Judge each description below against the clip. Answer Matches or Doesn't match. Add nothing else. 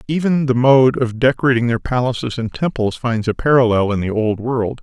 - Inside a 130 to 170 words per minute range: Doesn't match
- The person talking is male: Matches